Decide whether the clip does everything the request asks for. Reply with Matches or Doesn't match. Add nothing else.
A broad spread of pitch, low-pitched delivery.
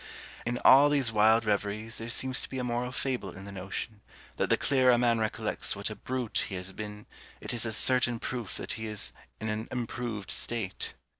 Doesn't match